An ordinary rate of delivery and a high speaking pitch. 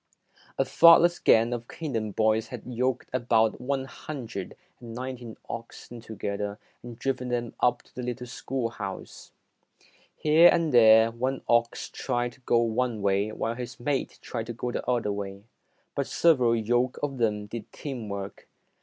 No: average, 160 wpm; low, 120 Hz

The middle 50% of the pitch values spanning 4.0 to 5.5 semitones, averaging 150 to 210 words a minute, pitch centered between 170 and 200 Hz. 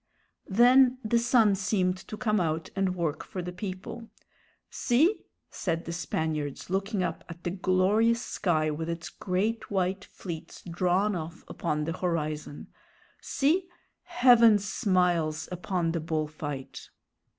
No: average, 4.4 semitones; slow, 135 wpm; medium, 185 Hz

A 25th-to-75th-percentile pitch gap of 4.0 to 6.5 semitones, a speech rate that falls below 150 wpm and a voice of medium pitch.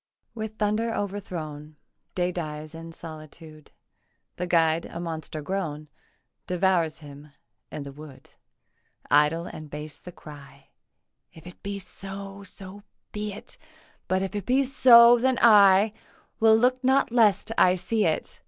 Yes: average, 5.2 semitones; average, 140 wpm; medium, 180 Hz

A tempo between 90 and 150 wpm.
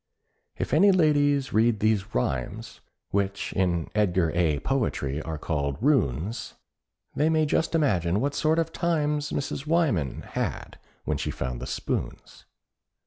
Yes: average, 140 wpm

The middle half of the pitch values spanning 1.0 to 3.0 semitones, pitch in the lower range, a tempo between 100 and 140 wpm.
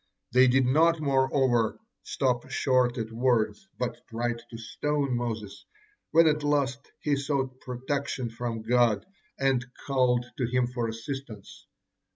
Yes: narrow, 2.6 semitones; low, 125 Hz; slow, 135 wpm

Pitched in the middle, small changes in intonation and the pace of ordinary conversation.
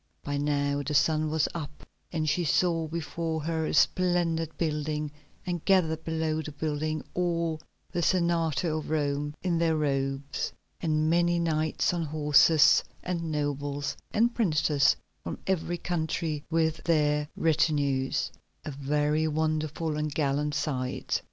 No: medium, 155 Hz; narrow, 2.0 semitones; slow, 130 wpm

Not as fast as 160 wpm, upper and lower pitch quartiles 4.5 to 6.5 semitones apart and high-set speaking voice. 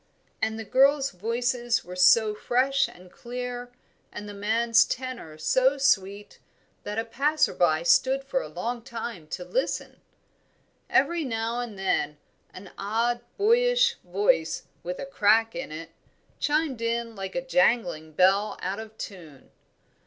Yes: average, 145 wpm; average, 5.1 semitones; high, 230 Hz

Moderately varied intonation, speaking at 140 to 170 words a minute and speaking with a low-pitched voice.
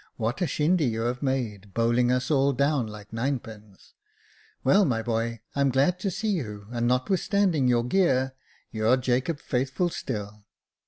Yes: average, 3.8 semitones; average, 155 wpm; low, 125 Hz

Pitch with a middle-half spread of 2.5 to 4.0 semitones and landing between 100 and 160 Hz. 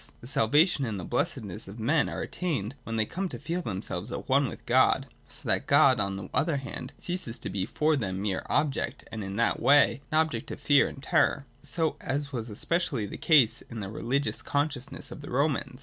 No: average, 5.3 semitones; low, 135 Hz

